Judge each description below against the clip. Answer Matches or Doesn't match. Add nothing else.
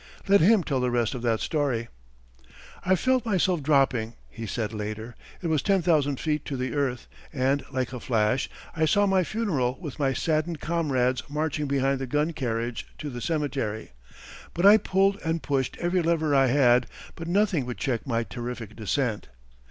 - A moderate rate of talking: Matches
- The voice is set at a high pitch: Doesn't match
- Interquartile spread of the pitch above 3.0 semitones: Matches